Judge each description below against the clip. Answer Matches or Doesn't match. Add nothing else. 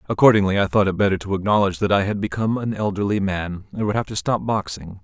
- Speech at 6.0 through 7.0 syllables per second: Matches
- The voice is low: Matches